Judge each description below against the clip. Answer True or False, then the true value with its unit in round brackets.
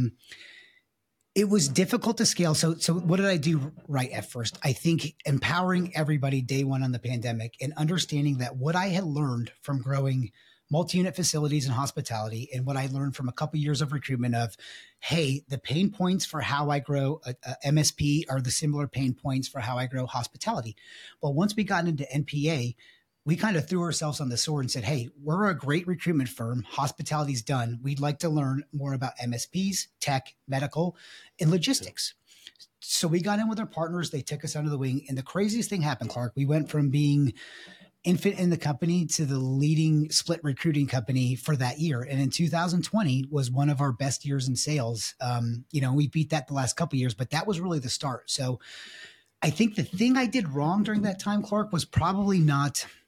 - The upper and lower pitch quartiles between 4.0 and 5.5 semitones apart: True (4.3 semitones)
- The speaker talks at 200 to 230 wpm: True (205 wpm)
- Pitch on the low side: False (145 Hz)